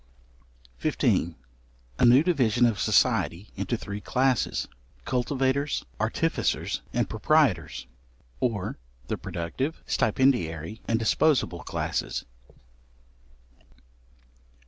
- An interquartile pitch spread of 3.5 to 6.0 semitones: Yes, average, 4.8 semitones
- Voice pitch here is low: Yes, low, 120 Hz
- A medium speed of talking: No, slow, 80 wpm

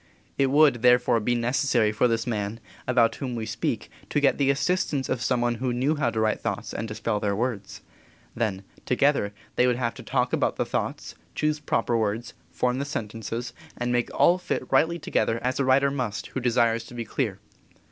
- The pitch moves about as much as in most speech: Yes, average, 3.0 semitones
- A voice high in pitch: No, low, 120 Hz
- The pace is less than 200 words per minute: No, fast, 205 wpm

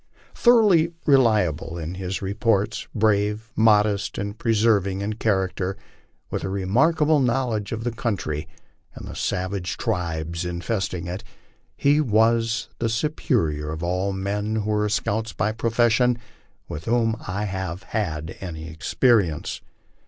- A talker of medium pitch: No, low, 105 Hz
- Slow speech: Yes, slow, 130 wpm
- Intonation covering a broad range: No, average, 4.0 semitones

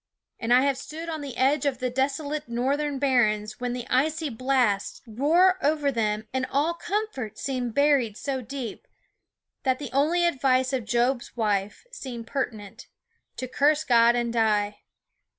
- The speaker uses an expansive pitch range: No, average, 3.5 semitones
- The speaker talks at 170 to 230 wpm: No, average, 155 wpm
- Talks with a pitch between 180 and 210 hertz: No, very high, 260 Hz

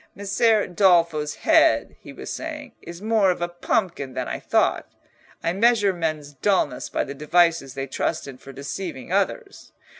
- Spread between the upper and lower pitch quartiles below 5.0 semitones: No, wide, 5.6 semitones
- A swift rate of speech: No, average, 160 wpm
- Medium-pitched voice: Yes, medium, 175 Hz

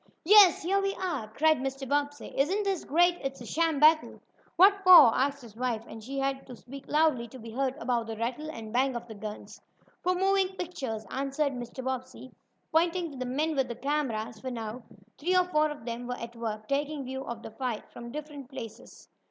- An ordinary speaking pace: No, fast, 210 wpm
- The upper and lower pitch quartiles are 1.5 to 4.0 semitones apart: No, average, 4.7 semitones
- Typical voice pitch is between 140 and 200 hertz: No, very high, 270 Hz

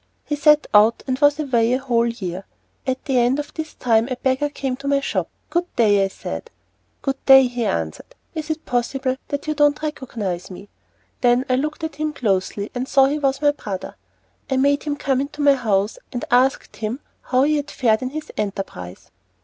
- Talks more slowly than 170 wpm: No, fast, 205 wpm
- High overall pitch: Yes, very high, 260 Hz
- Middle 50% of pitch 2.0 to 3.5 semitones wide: No, average, 4.2 semitones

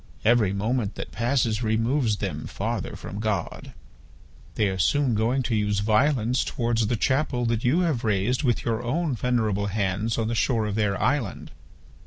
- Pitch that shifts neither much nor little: Yes, average, 3.0 semitones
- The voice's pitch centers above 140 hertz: No, low, 115 Hz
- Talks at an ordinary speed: Yes, average, 170 wpm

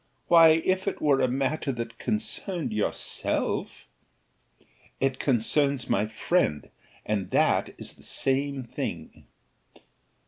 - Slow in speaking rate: Yes, slow, 115 wpm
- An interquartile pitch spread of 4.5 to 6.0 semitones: Yes, wide, 5.5 semitones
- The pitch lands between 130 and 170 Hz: Yes, low, 135 Hz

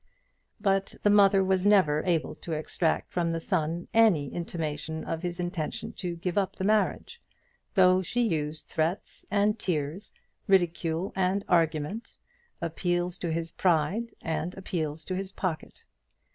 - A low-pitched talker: No, medium, 175 Hz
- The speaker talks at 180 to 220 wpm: No, average, 145 wpm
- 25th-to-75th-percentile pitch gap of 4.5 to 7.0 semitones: No, average, 3.2 semitones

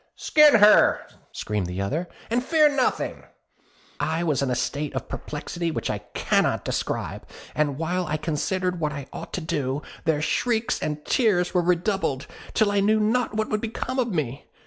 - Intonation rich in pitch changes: Yes, wide, 6.7 semitones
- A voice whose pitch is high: No, medium, 170 Hz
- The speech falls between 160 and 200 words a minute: Yes, average, 175 wpm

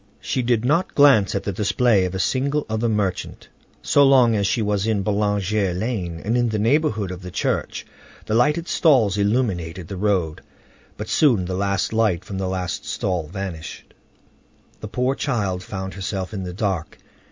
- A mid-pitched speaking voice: No, low, 100 Hz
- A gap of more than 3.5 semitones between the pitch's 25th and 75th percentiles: Yes, average, 4.1 semitones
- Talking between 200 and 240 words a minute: No, average, 175 wpm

